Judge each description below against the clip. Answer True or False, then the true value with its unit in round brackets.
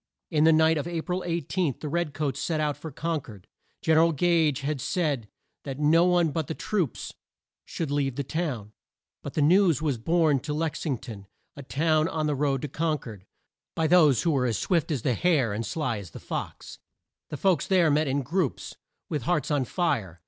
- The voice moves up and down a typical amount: True (3.6 semitones)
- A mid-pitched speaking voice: True (150 Hz)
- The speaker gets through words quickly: True (215 wpm)